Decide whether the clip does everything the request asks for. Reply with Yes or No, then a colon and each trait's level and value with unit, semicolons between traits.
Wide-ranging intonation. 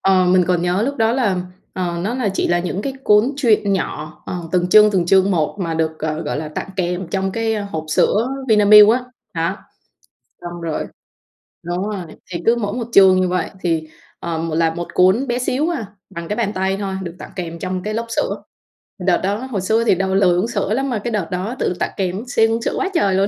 No: average, 3.9 semitones